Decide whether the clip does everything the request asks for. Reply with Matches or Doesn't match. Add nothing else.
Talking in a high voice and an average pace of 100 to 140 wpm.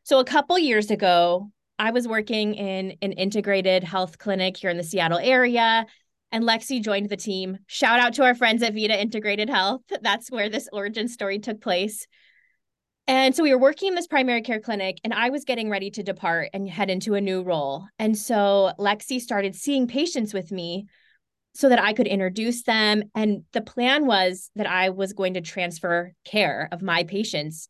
Doesn't match